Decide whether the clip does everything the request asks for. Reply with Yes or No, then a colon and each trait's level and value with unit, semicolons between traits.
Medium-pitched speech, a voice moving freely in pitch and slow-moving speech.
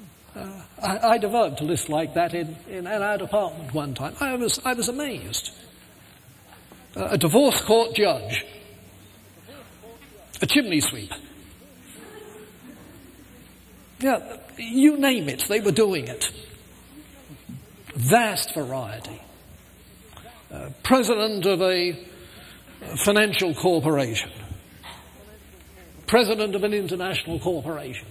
Yes: medium, 180 Hz; wide, 9.0 semitones; slow, 100 wpm